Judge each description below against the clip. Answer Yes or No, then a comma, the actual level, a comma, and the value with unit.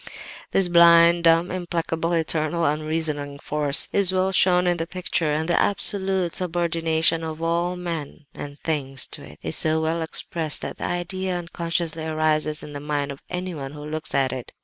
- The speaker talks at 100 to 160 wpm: No, average, 170 wpm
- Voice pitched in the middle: Yes, medium, 165 Hz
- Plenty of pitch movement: No, narrow, 2.4 semitones